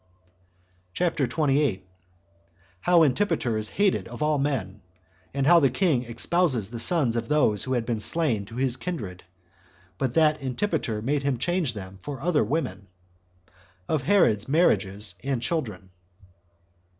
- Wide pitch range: Yes, wide, 6.2 semitones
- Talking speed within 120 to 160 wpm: Yes, average, 140 wpm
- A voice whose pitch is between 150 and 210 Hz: No, low, 135 Hz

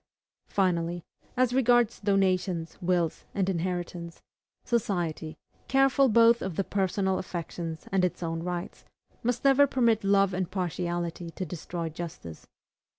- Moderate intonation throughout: Yes, average, 3.4 semitones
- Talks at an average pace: No, slow, 125 wpm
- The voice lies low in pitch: No, medium, 185 Hz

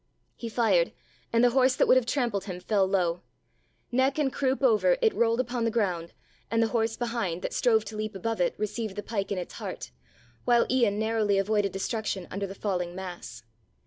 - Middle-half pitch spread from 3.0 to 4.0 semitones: Yes, average, 3.6 semitones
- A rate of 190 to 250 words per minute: Yes, average, 200 wpm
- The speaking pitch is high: Yes, high, 220 Hz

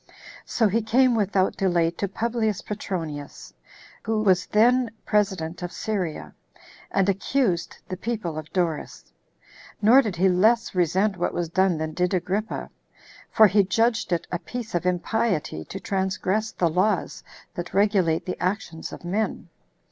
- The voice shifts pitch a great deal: No, average, 3.7 semitones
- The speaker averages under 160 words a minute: Yes, average, 150 wpm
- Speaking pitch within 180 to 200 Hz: Yes, high, 190 Hz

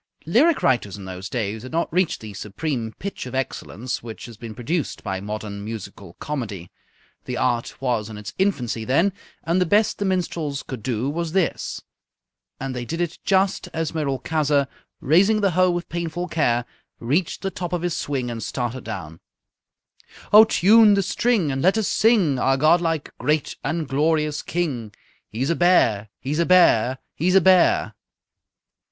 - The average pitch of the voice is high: No, medium, 145 Hz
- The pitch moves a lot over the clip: Yes, wide, 6.9 semitones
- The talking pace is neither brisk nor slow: Yes, average, 170 wpm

